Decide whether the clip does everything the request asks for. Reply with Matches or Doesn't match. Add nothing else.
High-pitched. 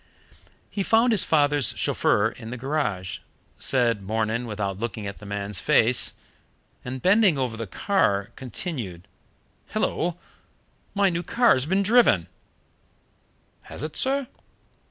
Doesn't match